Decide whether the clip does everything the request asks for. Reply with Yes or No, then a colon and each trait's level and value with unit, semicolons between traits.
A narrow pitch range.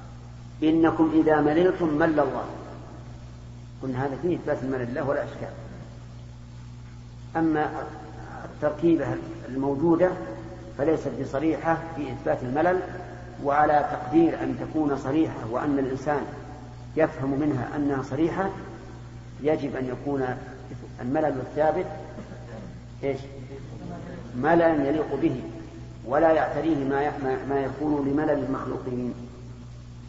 No: average, 4.1 semitones